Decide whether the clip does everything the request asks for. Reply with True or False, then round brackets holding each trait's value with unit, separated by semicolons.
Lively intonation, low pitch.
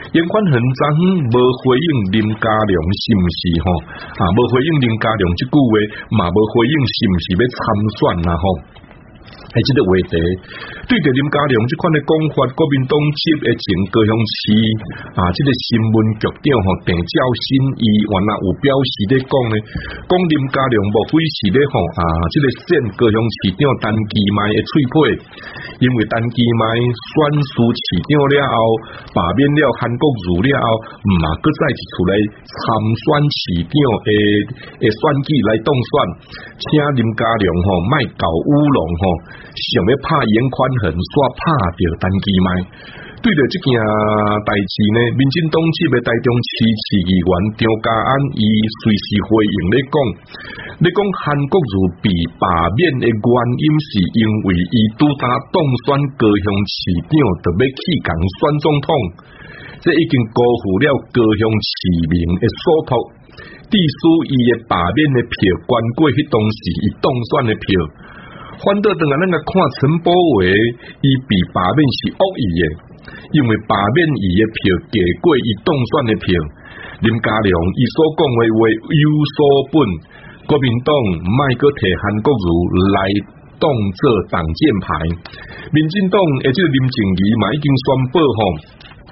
True (5.9 semitones; 115 Hz)